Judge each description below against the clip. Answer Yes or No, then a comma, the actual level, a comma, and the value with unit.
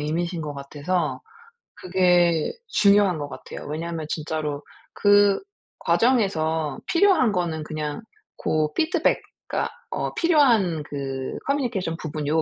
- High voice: No, medium, 165 Hz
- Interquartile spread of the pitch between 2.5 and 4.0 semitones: No, average, 5.0 semitones